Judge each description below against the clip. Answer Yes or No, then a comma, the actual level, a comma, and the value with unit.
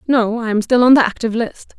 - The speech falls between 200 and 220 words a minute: No, fast, 270 wpm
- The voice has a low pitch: No, high, 230 Hz